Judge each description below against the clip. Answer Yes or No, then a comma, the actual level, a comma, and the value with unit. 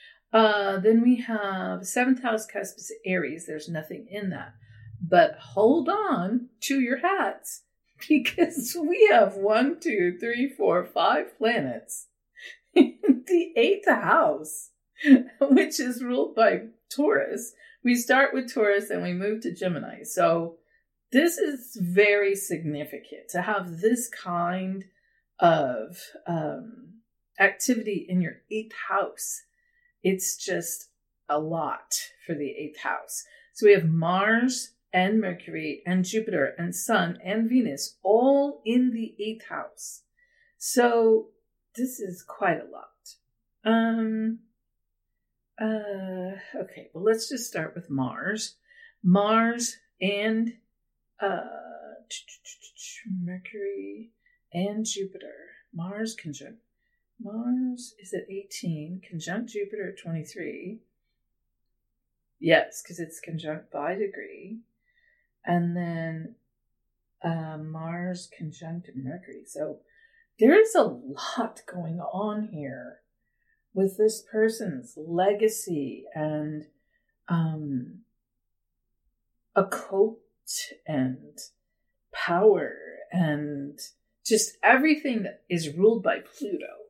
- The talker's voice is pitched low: No, high, 220 Hz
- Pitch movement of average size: No, wide, 6.6 semitones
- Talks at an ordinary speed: No, slow, 105 wpm